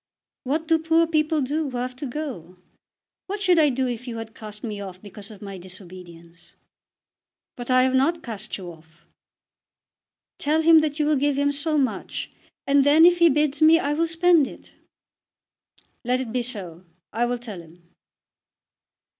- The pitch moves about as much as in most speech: No, wide, 6.9 semitones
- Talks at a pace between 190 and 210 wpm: No, average, 180 wpm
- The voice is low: No, very high, 260 Hz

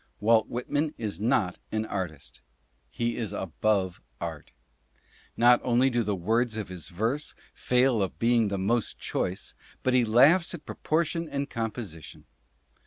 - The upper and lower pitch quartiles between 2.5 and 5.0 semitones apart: Yes, average, 4.1 semitones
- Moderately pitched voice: No, low, 115 Hz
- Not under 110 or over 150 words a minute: Yes, average, 145 wpm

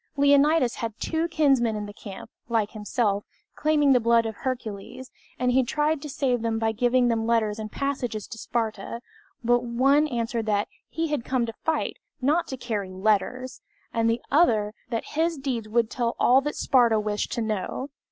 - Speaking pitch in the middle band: No, high, 235 Hz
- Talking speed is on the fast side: No, average, 180 wpm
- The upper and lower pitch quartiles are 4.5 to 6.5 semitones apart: No, average, 3.5 semitones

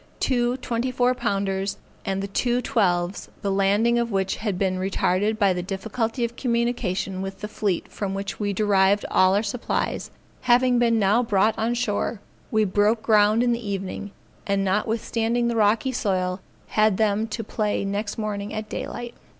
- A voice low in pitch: No, high, 210 Hz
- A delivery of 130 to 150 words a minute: No, average, 170 wpm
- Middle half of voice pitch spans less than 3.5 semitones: Yes, average, 3.1 semitones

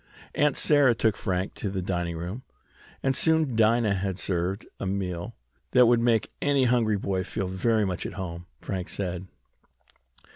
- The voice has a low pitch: Yes, low, 100 Hz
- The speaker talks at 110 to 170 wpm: Yes, average, 160 wpm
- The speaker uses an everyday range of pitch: Yes, average, 4.3 semitones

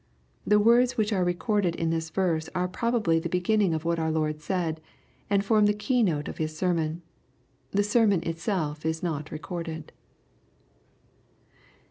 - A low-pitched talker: No, medium, 175 Hz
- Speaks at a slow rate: No, average, 155 wpm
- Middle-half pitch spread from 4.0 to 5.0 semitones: Yes, average, 4.4 semitones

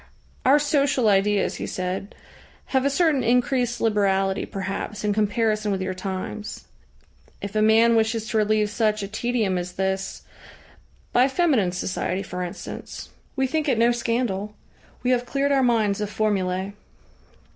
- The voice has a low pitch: No, high, 215 Hz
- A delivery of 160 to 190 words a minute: No, average, 150 wpm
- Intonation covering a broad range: No, average, 3.9 semitones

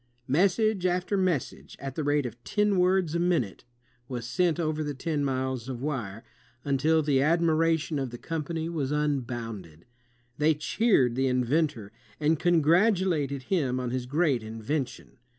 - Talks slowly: No, average, 150 wpm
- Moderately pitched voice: Yes, medium, 150 Hz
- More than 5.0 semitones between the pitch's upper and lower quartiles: No, average, 4.7 semitones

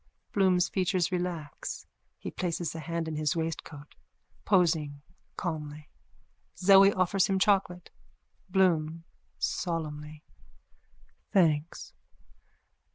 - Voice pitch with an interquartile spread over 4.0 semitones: No, average, 3.2 semitones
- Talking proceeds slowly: Yes, slow, 90 wpm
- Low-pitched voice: No, medium, 170 Hz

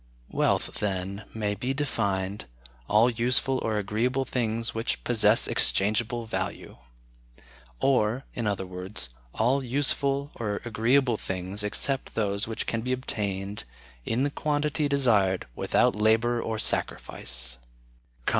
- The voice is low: Yes, low, 110 Hz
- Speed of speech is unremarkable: No, slow, 120 wpm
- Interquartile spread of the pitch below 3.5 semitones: No, average, 3.8 semitones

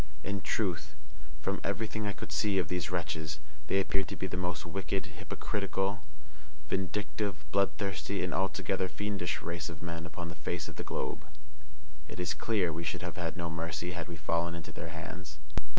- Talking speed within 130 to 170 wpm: No, average, 180 wpm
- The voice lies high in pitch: No, very low, 90 Hz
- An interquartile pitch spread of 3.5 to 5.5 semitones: No, average, 2.7 semitones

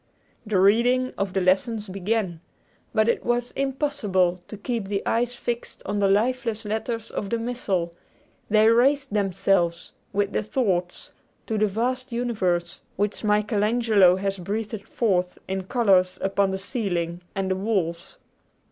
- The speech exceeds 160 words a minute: No, average, 150 wpm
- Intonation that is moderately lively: Yes, average, 3.6 semitones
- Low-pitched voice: No, high, 205 Hz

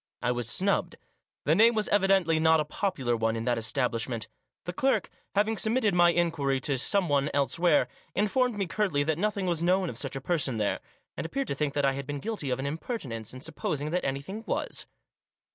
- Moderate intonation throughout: No, wide, 6.4 semitones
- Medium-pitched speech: Yes, medium, 160 Hz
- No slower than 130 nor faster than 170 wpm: No, fast, 205 wpm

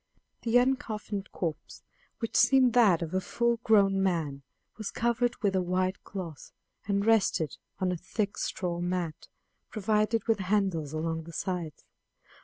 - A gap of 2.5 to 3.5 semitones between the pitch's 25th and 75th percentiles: No, average, 4.2 semitones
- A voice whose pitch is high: Yes, high, 195 Hz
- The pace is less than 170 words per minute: Yes, average, 145 wpm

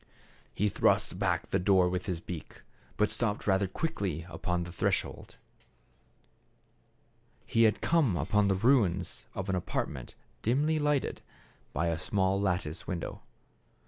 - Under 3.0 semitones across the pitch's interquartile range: No, average, 3.4 semitones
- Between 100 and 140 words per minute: Yes, slow, 135 wpm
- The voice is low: Yes, very low, 95 Hz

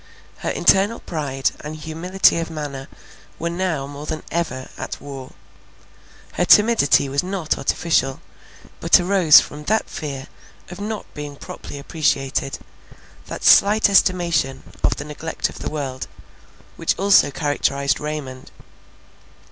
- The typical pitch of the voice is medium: Yes, medium, 150 Hz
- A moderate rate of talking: No, slow, 130 wpm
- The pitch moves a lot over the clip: No, average, 4.2 semitones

